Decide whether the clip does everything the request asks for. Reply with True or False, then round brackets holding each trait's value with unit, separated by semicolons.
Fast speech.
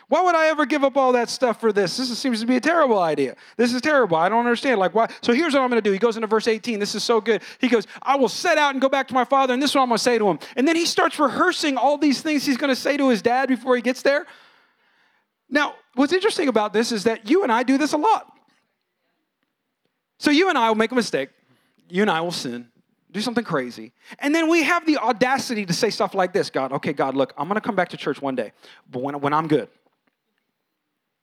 True (275 wpm)